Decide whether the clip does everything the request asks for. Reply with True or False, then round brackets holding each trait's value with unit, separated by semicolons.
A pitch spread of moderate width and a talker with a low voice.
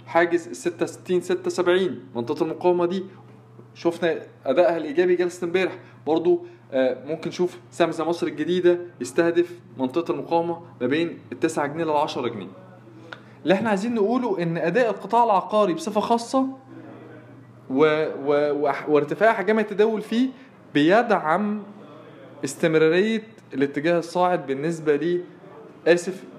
False (3.6 semitones; 170 Hz)